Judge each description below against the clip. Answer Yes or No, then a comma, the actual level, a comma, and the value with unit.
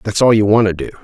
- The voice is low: Yes, low, 105 Hz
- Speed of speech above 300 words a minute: Yes, fast, 350 wpm